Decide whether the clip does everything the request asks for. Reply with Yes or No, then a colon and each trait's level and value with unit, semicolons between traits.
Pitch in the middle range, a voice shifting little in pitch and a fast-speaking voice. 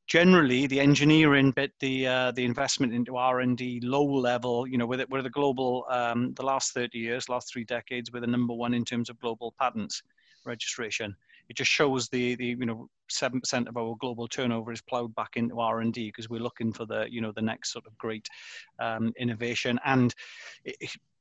No: low, 120 Hz; narrow, 1.8 semitones; fast, 215 wpm